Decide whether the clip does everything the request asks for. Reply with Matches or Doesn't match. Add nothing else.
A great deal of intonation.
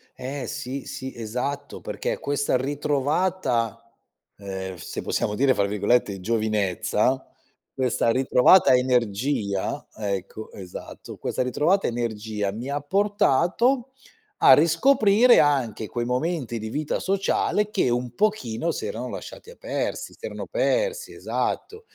Matches